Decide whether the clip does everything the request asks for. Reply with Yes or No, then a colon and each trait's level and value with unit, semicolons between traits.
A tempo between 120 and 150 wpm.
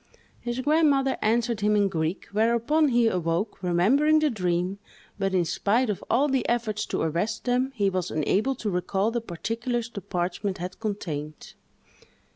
No: average, 160 wpm